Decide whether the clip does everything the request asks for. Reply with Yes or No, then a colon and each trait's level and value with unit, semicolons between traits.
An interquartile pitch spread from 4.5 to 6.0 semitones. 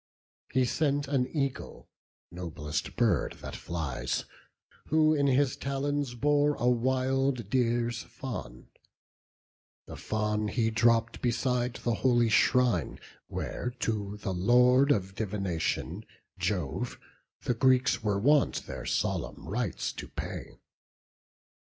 No: average, 4.1 semitones